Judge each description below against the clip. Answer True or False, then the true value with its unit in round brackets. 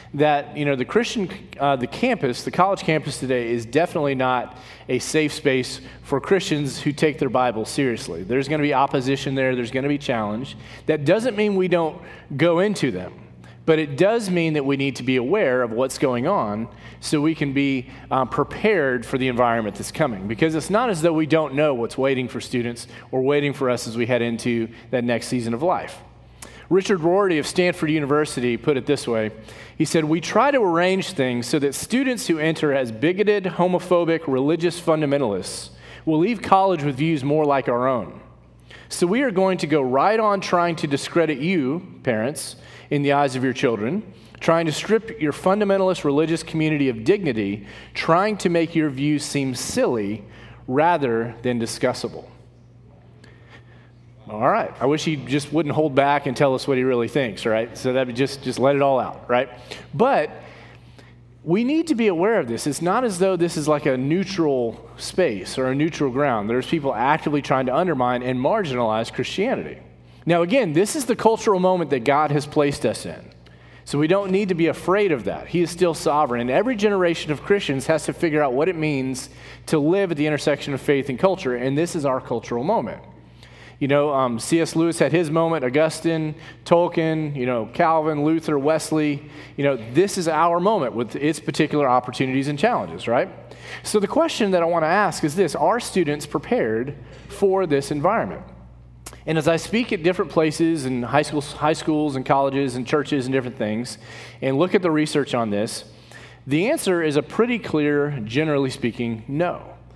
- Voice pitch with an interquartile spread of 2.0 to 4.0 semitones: False (4.7 semitones)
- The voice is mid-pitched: True (145 Hz)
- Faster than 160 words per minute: True (195 wpm)